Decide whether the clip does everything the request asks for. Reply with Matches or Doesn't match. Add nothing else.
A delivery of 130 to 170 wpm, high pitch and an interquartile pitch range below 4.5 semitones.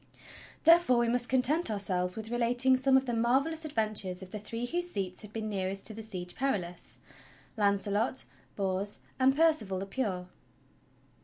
Doesn't match